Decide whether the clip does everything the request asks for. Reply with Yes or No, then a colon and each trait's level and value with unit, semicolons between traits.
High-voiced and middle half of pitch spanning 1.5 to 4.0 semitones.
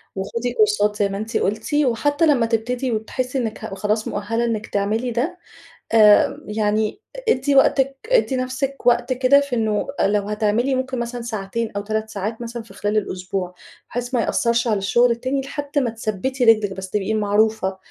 Yes: high, 230 Hz; average, 3.4 semitones